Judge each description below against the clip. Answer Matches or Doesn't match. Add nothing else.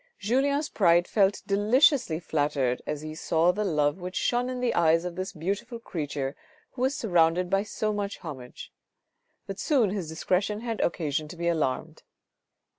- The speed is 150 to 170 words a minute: Matches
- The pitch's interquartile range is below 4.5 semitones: Doesn't match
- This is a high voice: Doesn't match